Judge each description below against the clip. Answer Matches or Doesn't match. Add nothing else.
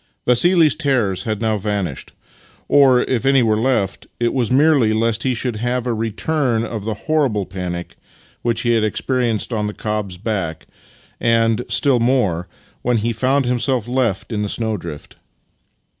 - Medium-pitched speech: Doesn't match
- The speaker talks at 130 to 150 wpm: Doesn't match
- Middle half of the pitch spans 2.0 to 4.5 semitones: Matches